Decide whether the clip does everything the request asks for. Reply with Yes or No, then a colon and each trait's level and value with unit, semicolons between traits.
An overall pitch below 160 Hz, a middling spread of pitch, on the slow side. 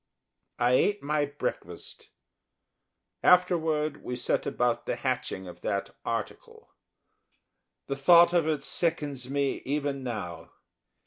Yes: medium, 140 Hz; average, 4.4 semitones; slow, 115 wpm